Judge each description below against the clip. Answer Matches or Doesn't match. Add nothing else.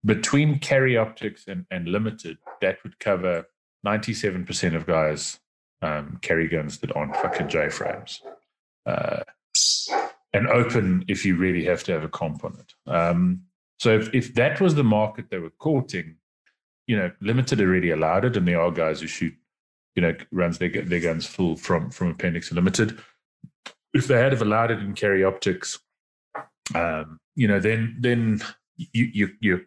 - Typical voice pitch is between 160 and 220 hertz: Doesn't match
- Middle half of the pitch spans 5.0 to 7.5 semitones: Matches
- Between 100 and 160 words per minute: Doesn't match